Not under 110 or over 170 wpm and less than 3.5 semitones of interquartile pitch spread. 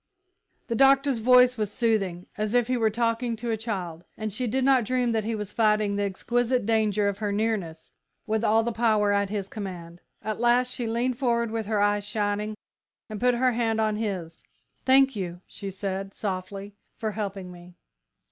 No: average, 190 wpm; average, 2.8 semitones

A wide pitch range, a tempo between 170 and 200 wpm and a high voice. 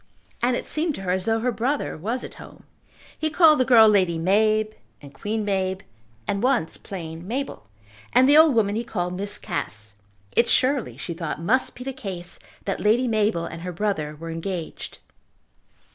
Yes: wide, 5.9 semitones; average, 185 wpm; high, 205 Hz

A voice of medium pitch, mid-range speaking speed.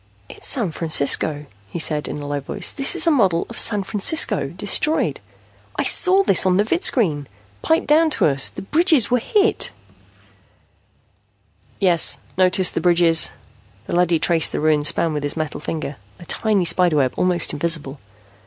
Yes: medium, 175 Hz; average, 170 wpm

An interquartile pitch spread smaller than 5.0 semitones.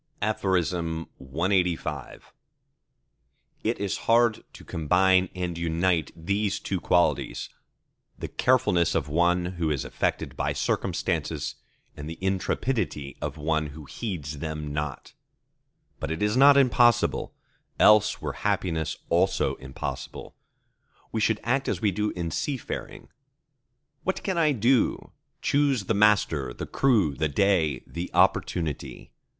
No: average, 5.3 semitones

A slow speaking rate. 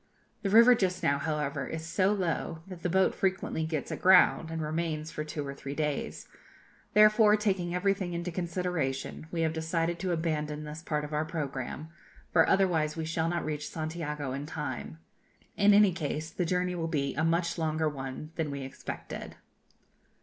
No: average, 175 wpm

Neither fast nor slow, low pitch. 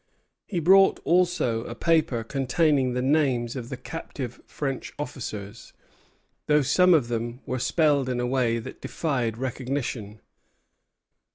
No: slow, 130 wpm; low, 130 Hz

